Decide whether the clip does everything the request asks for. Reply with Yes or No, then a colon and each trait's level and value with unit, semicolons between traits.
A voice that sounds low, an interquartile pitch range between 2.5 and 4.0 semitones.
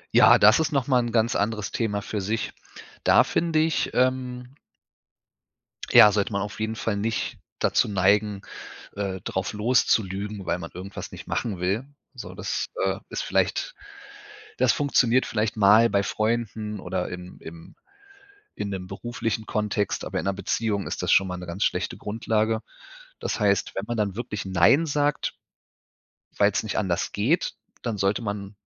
Yes: low, 105 Hz; average, 2.8 semitones